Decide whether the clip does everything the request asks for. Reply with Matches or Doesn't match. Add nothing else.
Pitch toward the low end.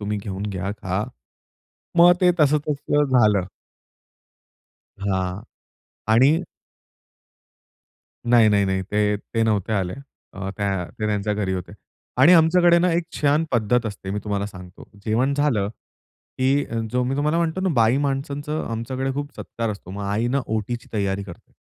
Matches